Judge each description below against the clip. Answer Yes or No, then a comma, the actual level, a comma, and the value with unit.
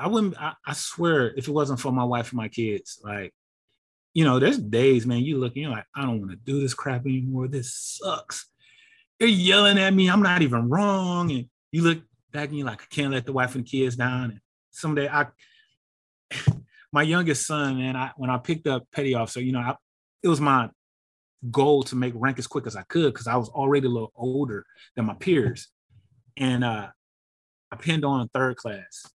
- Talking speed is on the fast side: Yes, fast, 220 wpm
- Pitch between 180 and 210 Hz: No, low, 135 Hz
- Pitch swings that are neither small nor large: Yes, average, 3.5 semitones